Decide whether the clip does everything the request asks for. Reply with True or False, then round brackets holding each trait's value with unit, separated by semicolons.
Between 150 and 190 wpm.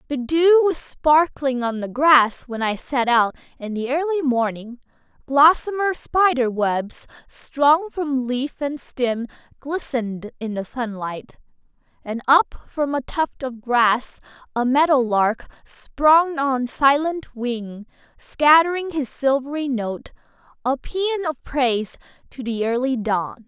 False (135 wpm)